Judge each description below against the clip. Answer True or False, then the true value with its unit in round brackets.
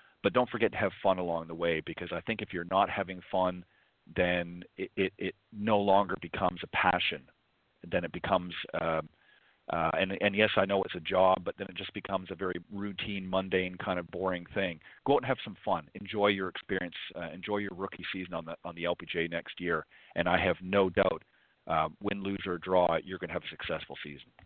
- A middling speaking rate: False (220 wpm)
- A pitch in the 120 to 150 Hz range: False (95 Hz)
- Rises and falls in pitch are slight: True (2.1 semitones)